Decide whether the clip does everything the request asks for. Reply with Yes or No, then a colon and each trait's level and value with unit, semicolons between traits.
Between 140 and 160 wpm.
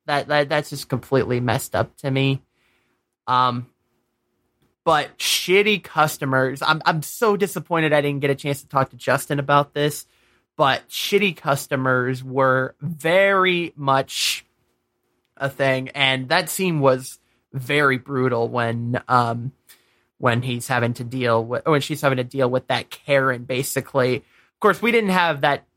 Yes: average, 150 wpm